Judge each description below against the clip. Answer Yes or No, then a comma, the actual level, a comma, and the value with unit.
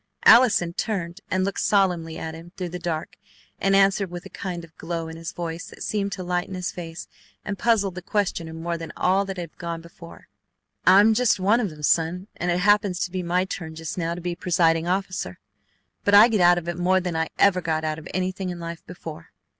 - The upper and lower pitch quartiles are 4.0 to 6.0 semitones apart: No, narrow, 2.4 semitones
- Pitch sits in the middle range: Yes, medium, 175 Hz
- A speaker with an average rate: No, fast, 225 wpm